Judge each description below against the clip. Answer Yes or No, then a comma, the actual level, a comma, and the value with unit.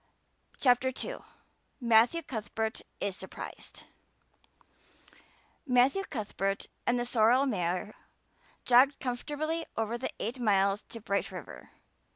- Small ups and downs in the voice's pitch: No, average, 3.7 semitones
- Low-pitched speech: No, high, 240 Hz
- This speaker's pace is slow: Yes, slow, 105 wpm